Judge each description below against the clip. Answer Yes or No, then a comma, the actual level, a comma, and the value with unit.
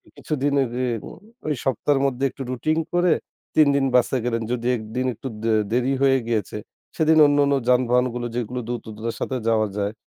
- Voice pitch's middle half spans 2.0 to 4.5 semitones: Yes, average, 3.1 semitones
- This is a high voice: No, low, 125 Hz